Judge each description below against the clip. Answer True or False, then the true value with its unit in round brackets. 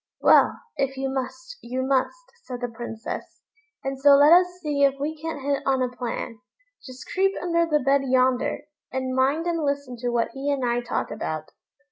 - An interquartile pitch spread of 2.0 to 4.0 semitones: True (2.9 semitones)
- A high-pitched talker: True (270 Hz)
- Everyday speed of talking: True (190 wpm)